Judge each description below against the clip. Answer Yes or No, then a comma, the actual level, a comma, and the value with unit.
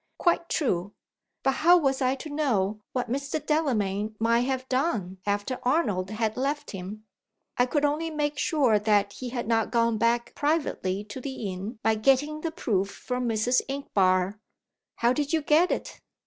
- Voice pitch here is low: No, high, 245 Hz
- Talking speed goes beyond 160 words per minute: Yes, average, 170 wpm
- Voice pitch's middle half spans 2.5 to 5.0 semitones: No, wide, 5.4 semitones